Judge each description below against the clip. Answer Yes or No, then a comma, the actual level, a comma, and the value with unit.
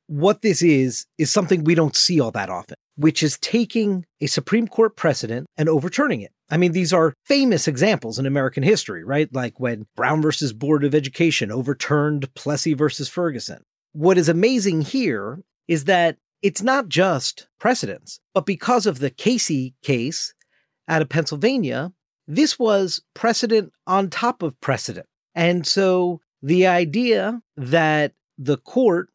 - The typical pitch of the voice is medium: Yes, medium, 165 Hz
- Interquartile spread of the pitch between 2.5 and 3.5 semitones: No, average, 5.0 semitones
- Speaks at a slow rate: No, average, 155 wpm